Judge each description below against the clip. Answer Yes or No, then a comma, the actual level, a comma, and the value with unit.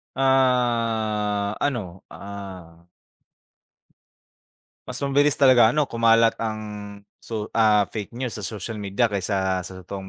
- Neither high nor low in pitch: No, low, 110 Hz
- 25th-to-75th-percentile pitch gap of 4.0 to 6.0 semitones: No, average, 3.1 semitones